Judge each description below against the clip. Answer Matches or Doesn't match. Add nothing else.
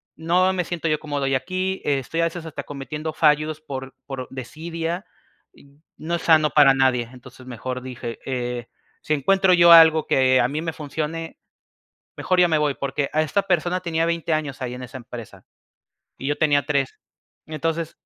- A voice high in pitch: Doesn't match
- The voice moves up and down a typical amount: Matches